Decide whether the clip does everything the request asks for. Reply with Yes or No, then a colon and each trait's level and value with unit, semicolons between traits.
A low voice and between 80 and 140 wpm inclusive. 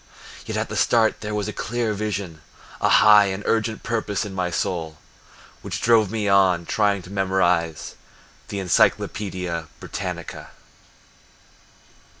Yes: low, 100 Hz; slow, 135 wpm